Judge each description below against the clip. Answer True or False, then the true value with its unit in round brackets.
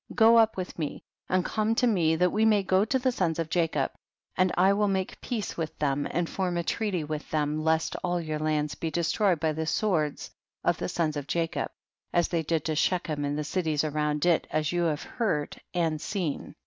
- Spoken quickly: True (215 wpm)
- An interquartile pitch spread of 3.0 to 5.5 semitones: True (3.5 semitones)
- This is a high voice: False (165 Hz)